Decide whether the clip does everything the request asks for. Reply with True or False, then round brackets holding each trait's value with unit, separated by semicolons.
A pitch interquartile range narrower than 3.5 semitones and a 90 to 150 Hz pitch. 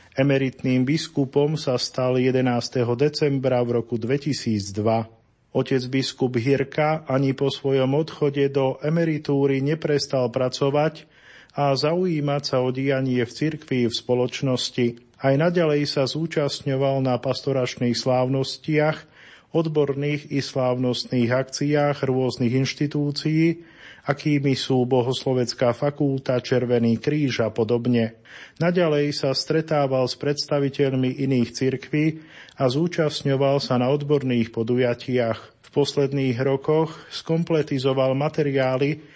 True (2.6 semitones; 135 Hz)